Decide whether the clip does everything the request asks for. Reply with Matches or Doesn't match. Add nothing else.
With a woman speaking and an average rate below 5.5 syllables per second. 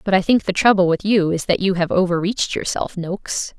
Doesn't match